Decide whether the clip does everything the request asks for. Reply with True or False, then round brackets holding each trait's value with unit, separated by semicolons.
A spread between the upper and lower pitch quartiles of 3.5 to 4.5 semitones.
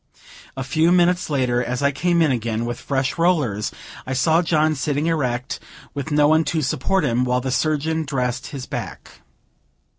True (4.1 semitones)